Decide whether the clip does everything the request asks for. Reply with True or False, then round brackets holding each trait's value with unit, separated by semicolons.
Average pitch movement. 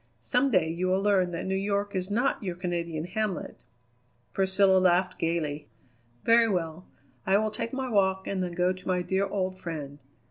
False (2.3 semitones)